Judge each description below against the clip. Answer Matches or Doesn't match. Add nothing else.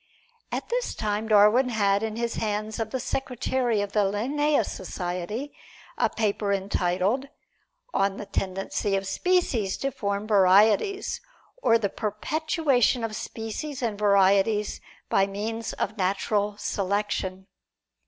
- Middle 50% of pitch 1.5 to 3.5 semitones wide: Matches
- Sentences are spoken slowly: Matches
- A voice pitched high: Matches